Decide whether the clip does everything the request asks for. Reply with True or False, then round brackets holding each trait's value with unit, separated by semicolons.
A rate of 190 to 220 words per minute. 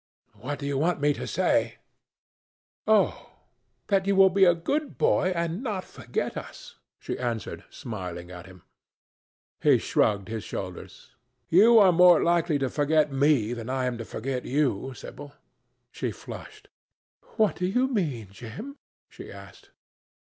False (150 wpm)